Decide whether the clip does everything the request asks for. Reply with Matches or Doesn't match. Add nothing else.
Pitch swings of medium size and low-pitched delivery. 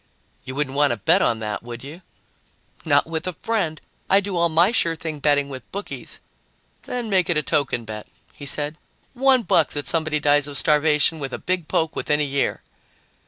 Doesn't match